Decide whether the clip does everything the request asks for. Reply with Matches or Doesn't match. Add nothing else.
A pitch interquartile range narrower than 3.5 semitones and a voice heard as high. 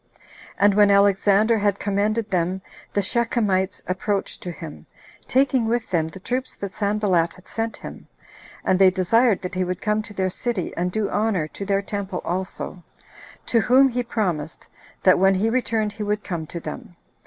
Matches